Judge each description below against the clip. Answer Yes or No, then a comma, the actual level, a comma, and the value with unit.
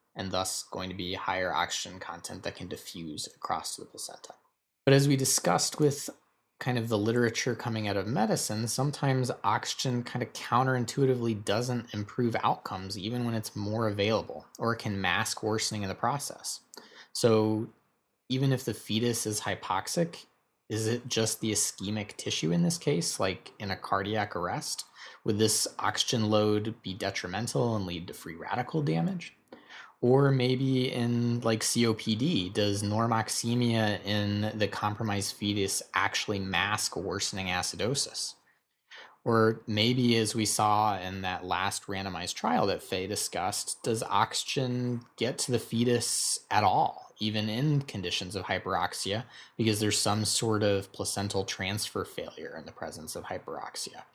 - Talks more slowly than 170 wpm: Yes, average, 150 wpm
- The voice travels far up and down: No, average, 2.9 semitones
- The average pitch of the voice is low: Yes, low, 110 Hz